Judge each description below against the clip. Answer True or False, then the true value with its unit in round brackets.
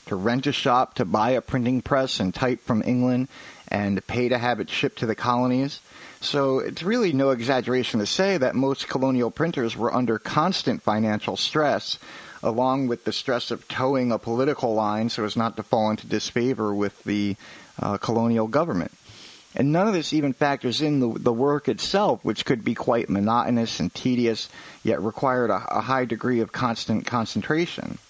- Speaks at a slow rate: False (185 wpm)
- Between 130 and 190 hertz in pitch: False (120 Hz)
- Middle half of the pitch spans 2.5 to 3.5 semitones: True (2.9 semitones)